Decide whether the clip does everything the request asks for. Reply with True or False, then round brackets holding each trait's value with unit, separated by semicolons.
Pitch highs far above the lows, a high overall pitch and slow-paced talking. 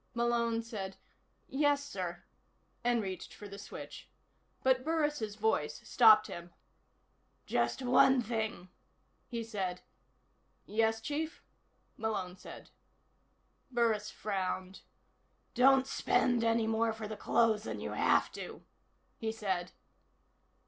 False (3.5 semitones; 220 Hz; 110 wpm)